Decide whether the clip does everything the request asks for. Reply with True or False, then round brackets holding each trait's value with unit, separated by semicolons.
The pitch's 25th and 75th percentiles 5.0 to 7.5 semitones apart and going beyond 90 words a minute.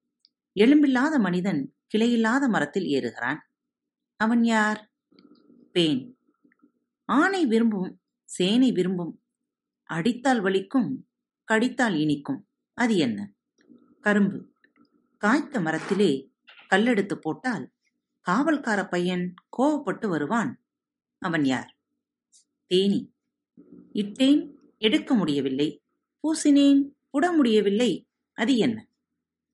False (5.6 semitones; 75 wpm)